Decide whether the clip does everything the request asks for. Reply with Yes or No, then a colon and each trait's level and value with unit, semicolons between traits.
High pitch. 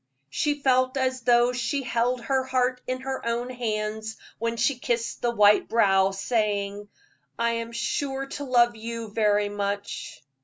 Yes: high, 235 Hz